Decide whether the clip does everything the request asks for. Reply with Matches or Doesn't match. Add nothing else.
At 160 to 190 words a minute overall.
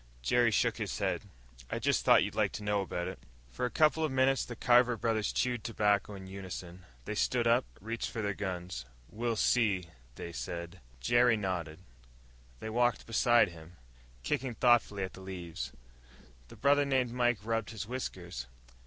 Matches